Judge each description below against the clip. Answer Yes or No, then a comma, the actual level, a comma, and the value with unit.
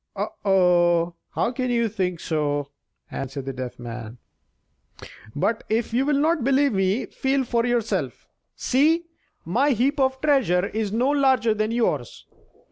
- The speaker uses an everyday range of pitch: No, wide, 7.3 semitones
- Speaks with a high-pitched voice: Yes, high, 225 Hz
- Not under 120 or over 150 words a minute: Yes, average, 145 wpm